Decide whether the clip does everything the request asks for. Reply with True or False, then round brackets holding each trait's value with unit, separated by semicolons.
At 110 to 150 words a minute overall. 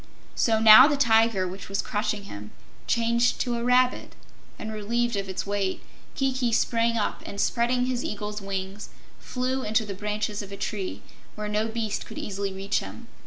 False (175 wpm)